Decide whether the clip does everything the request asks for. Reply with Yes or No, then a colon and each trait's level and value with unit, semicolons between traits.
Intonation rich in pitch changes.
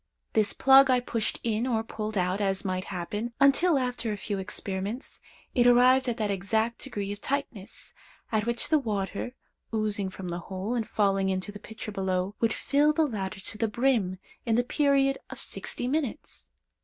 No: average, 4.2 semitones